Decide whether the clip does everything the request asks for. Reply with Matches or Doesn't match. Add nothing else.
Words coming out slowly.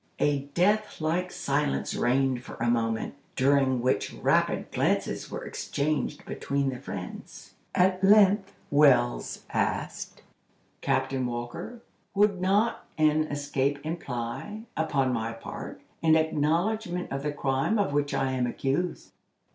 Matches